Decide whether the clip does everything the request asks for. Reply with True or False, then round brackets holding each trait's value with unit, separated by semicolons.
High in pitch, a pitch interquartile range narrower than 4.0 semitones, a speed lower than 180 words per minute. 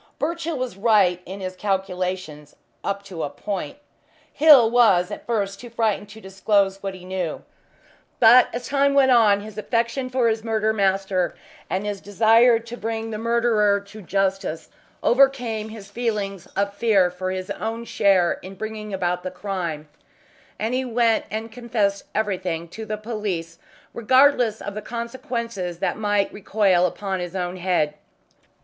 True (205 Hz; 3.5 semitones; 155 wpm)